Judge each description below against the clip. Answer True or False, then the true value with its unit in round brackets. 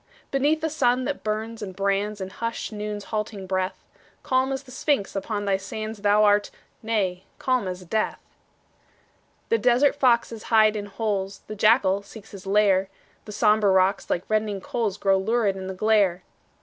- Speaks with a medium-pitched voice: False (210 Hz)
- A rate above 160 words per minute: True (170 wpm)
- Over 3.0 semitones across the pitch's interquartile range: False (2.7 semitones)